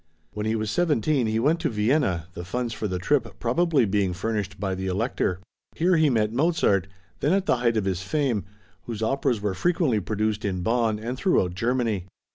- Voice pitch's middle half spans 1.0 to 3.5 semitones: No, average, 5.1 semitones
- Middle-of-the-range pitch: No, low, 110 Hz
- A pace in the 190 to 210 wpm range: Yes, average, 195 wpm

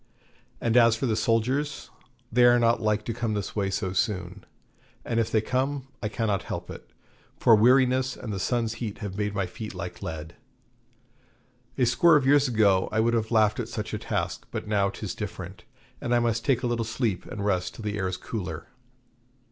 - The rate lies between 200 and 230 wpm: Yes, fast, 205 wpm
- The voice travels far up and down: No, average, 2.8 semitones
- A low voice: Yes, low, 110 Hz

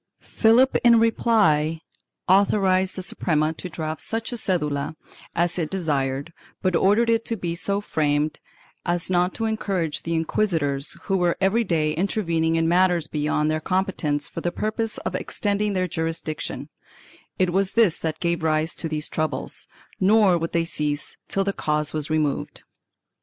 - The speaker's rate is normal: Yes, average, 165 wpm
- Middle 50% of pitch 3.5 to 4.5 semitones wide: Yes, average, 4.0 semitones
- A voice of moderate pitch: Yes, medium, 170 Hz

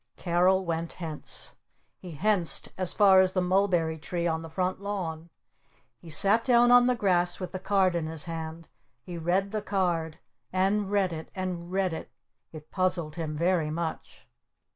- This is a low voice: No, medium, 180 Hz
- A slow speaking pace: No, average, 170 wpm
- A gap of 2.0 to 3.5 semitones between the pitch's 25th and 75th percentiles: Yes, average, 2.8 semitones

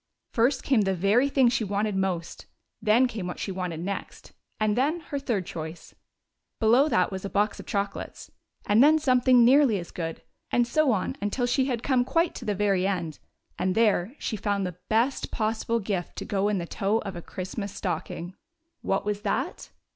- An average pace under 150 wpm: No, average, 190 wpm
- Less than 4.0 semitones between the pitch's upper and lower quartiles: No, average, 4.4 semitones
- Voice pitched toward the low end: No, high, 210 Hz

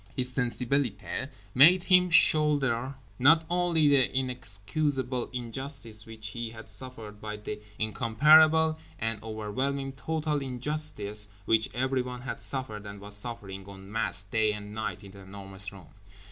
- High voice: No, low, 120 Hz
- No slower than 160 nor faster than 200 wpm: No, slow, 135 wpm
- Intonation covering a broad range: No, average, 4.7 semitones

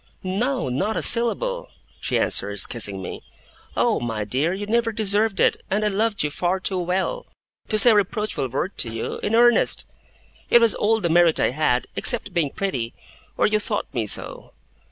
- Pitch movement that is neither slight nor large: No, wide, 7.9 semitones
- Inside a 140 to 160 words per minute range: No, average, 185 wpm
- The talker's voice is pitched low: No, high, 195 Hz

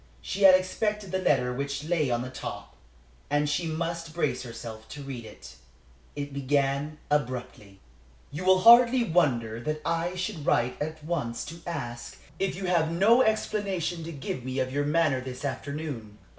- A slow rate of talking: No, average, 170 wpm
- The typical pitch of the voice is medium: Yes, medium, 150 Hz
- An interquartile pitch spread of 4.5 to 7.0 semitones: Yes, average, 5.2 semitones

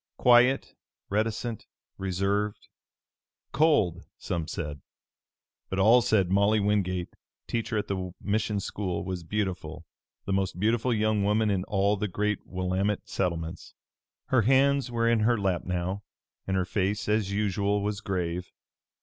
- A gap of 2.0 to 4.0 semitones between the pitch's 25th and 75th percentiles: Yes, average, 2.7 semitones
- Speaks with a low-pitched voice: Yes, low, 100 Hz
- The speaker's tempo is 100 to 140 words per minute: Yes, slow, 135 wpm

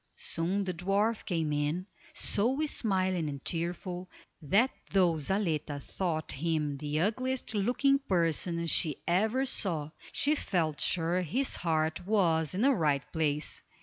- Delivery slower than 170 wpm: Yes, slow, 135 wpm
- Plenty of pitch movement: No, average, 4.4 semitones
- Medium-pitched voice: Yes, medium, 175 Hz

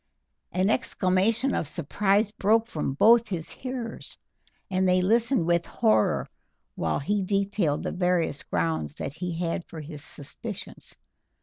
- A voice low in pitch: No, medium, 185 Hz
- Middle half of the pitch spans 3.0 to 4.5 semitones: No, average, 5.2 semitones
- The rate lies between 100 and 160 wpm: Yes, slow, 135 wpm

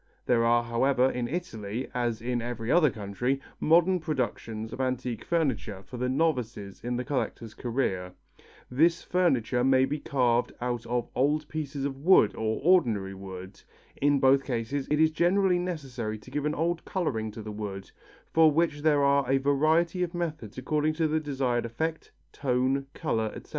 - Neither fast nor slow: Yes, average, 170 wpm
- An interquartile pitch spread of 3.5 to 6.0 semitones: Yes, average, 4.8 semitones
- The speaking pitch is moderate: No, low, 130 Hz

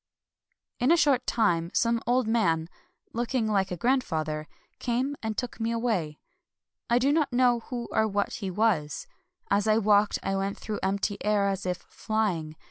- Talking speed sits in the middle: Yes, average, 185 wpm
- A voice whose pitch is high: Yes, high, 215 Hz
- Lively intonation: No, average, 4.0 semitones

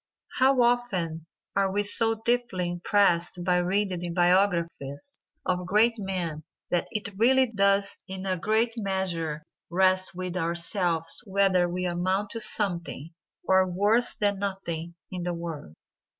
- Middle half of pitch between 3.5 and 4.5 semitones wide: No, average, 2.8 semitones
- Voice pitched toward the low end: No, medium, 185 Hz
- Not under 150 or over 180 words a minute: No, slow, 135 wpm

